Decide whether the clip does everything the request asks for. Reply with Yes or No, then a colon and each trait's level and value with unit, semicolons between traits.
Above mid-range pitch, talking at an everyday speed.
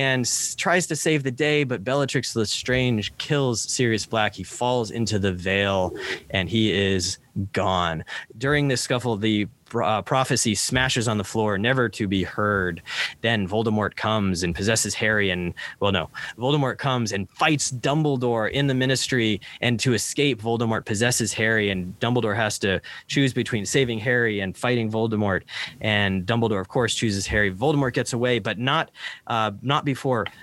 No: low, 115 Hz; average, 165 wpm